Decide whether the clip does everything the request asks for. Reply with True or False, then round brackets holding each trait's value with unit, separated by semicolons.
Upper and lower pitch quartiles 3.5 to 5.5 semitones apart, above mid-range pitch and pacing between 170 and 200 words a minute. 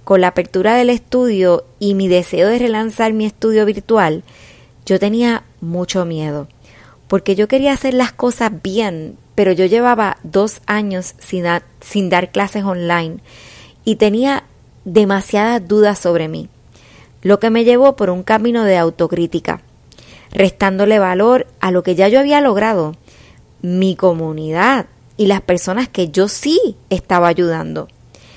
False (3.8 semitones; 195 Hz; 145 wpm)